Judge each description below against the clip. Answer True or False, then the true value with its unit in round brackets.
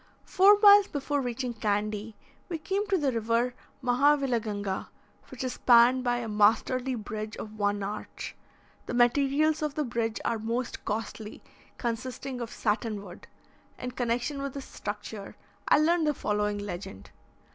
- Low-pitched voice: False (240 Hz)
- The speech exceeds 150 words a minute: False (145 wpm)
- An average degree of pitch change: True (4.5 semitones)